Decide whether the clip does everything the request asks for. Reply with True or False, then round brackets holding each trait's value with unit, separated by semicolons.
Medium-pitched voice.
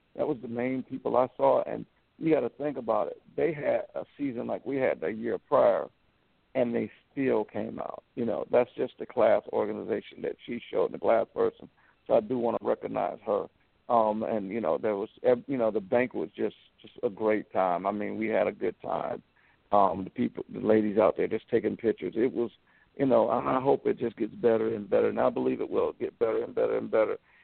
False (125 Hz)